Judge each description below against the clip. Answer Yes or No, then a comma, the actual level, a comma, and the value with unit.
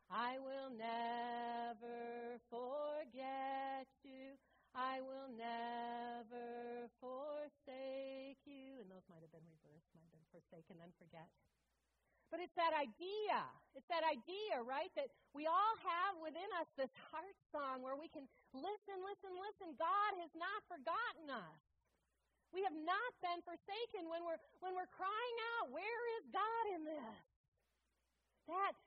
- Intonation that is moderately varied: No, wide, 6.9 semitones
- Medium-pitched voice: No, very high, 275 Hz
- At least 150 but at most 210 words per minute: No, average, 140 wpm